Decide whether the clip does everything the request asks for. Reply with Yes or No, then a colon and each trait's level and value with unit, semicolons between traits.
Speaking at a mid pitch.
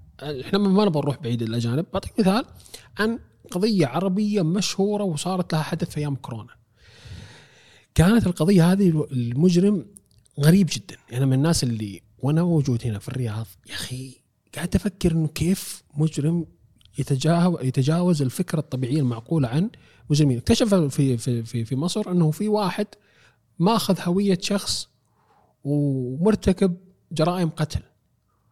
Yes: medium, 155 Hz